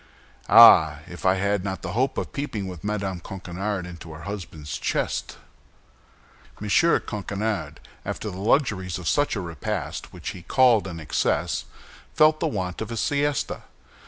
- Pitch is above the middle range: No, very low, 95 Hz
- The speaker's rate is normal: Yes, average, 155 wpm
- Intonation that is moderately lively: Yes, average, 3.6 semitones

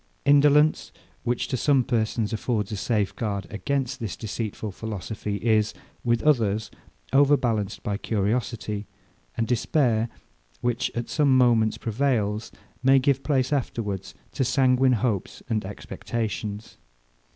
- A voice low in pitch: Yes, low, 115 Hz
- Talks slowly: Yes, slow, 120 wpm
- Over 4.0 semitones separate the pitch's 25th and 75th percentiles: No, average, 3.6 semitones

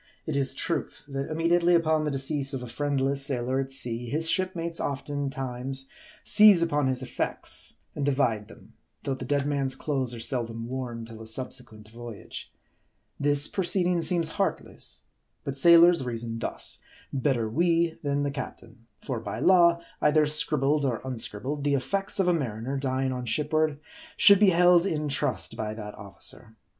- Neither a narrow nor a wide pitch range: Yes, average, 4.2 semitones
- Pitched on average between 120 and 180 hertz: Yes, medium, 140 Hz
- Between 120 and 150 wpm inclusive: No, average, 160 wpm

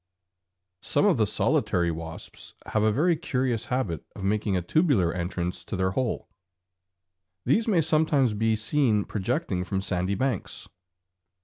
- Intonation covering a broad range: Yes, wide, 6.2 semitones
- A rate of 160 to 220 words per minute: No, average, 140 wpm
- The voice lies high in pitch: No, low, 105 Hz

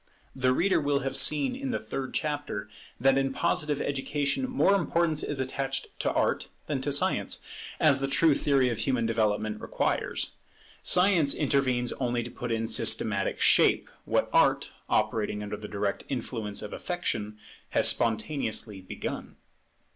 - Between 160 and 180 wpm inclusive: No, average, 150 wpm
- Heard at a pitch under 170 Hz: Yes, low, 135 Hz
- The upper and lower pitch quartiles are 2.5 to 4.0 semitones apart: No, average, 4.7 semitones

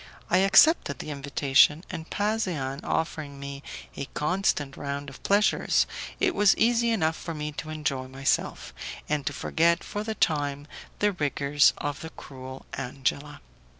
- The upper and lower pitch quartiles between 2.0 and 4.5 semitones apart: No, average, 4.9 semitones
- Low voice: No, medium, 150 Hz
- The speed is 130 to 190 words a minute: Yes, average, 150 wpm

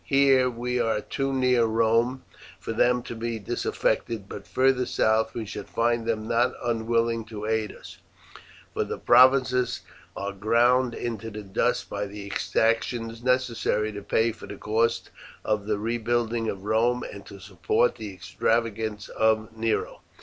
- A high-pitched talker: No, low, 115 Hz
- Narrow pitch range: Yes, narrow, 1.9 semitones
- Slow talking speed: No, average, 155 wpm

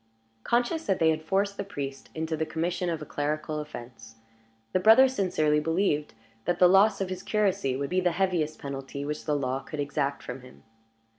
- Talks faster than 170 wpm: Yes, average, 195 wpm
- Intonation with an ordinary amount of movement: Yes, average, 4.6 semitones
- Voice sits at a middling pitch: Yes, medium, 160 Hz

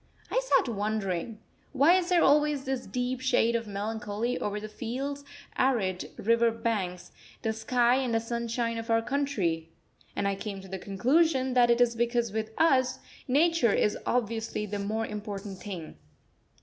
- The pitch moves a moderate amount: Yes, average, 3.7 semitones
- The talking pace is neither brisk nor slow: Yes, average, 160 wpm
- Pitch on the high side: Yes, high, 230 Hz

